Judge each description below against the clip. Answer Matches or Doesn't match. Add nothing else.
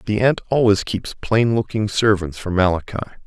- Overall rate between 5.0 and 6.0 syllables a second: Matches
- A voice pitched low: Matches